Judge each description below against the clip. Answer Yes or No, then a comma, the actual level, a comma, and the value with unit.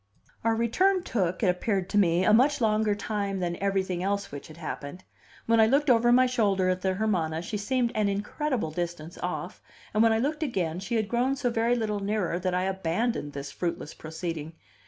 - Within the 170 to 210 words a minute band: Yes, average, 200 wpm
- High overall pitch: Yes, high, 200 Hz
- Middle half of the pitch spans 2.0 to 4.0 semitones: No, average, 4.5 semitones